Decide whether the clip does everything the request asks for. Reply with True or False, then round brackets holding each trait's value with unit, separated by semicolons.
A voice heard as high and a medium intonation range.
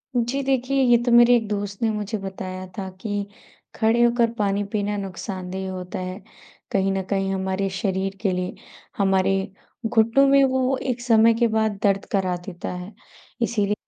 True (205 Hz; 3.5 semitones)